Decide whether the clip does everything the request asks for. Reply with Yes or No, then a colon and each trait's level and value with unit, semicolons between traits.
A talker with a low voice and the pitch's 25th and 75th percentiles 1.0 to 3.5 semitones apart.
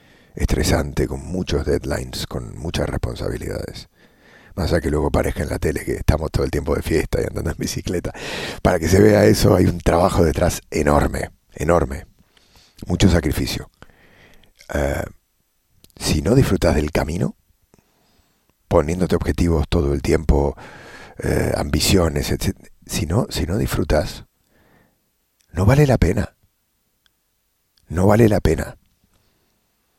No: very low, 90 Hz; average, 4.0 semitones